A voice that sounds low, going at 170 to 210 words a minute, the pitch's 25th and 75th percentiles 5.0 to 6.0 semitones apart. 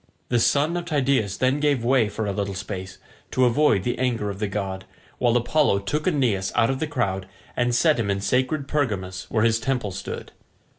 Yes: low, 120 Hz; average, 200 wpm; wide, 5.6 semitones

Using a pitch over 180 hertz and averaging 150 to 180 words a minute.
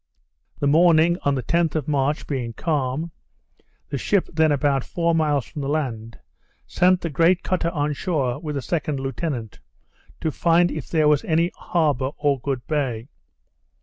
No: medium, 150 Hz; average, 165 wpm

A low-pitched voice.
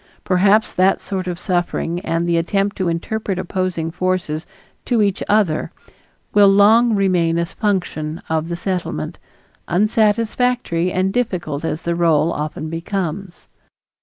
No: medium, 185 Hz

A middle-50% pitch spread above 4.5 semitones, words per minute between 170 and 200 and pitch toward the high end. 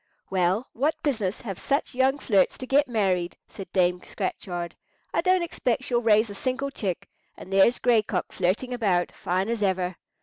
Yes: wide, 5.5 semitones; average, 175 wpm; high, 210 Hz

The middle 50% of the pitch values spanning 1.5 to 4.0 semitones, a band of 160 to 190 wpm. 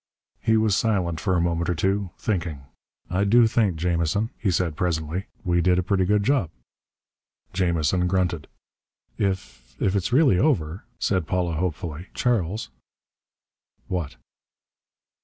No: average, 3.2 semitones; average, 140 wpm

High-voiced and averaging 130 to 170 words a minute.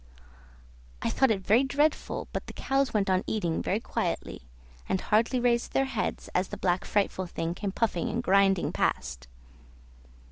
Yes: high, 210 Hz; average, 165 wpm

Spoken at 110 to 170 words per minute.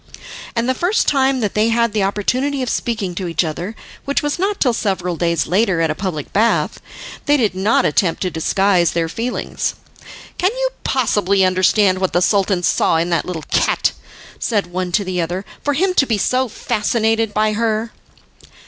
No: average, 185 wpm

